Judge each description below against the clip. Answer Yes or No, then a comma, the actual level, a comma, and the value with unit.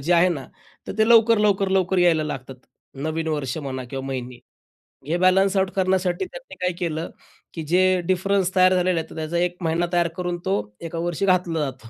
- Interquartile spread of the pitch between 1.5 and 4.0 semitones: Yes, average, 2.8 semitones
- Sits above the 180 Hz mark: No, medium, 175 Hz